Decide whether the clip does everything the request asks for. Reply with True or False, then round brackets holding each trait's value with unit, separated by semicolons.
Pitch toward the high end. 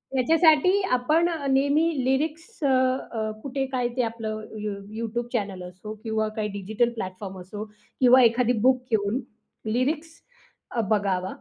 True (240 Hz)